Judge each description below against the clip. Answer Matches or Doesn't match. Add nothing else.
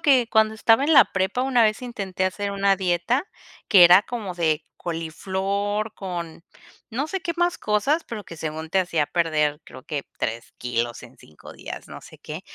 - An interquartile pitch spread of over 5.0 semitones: Matches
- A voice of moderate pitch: Doesn't match